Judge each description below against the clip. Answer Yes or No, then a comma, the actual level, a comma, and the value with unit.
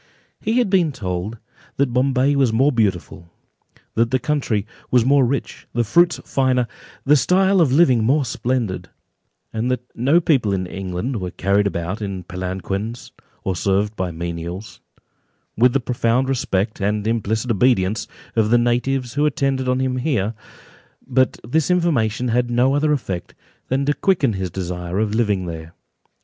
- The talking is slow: No, average, 160 wpm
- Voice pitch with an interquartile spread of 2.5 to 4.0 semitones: No, wide, 5.5 semitones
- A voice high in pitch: No, low, 120 Hz